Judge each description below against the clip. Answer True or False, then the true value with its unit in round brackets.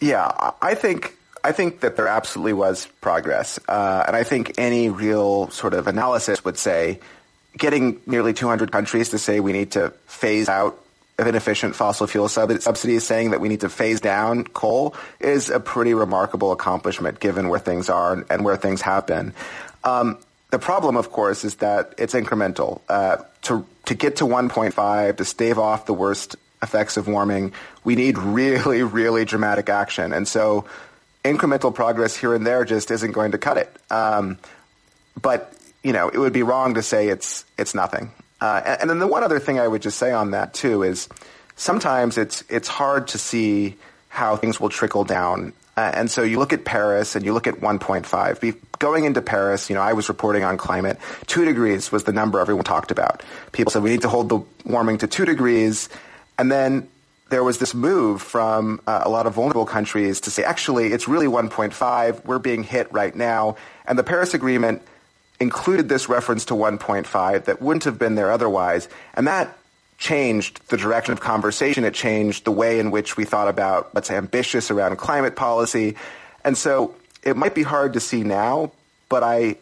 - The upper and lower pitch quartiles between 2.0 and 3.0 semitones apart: True (2.6 semitones)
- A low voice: True (110 Hz)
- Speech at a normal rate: True (190 wpm)